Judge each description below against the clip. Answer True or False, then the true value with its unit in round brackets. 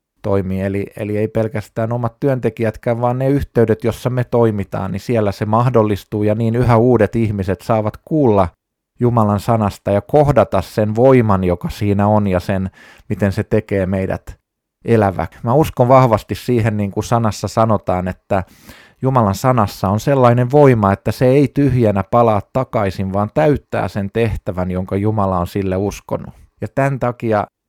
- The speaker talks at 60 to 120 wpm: False (155 wpm)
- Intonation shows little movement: False (3.4 semitones)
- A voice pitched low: True (110 Hz)